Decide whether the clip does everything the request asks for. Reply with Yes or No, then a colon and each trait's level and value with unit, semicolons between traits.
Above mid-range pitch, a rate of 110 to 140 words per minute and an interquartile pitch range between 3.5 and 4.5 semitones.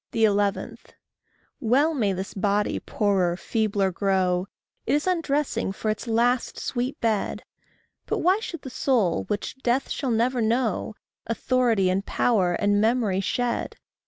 Yes: high, 220 Hz; slow, 135 wpm; average, 4.2 semitones